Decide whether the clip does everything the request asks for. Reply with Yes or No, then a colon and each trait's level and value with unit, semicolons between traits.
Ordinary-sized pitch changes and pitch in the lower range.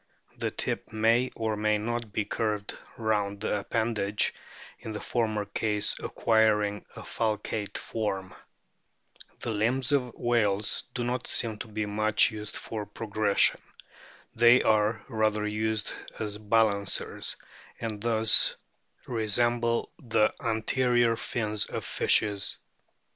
No: narrow, 1.6 semitones; low, 110 Hz